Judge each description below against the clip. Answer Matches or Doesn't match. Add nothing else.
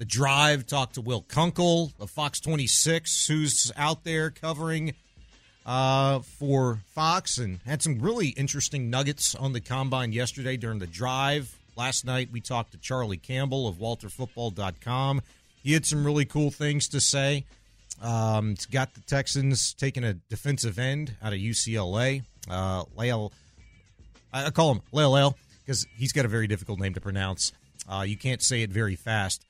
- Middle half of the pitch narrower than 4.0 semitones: Doesn't match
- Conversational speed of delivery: Matches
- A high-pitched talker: Doesn't match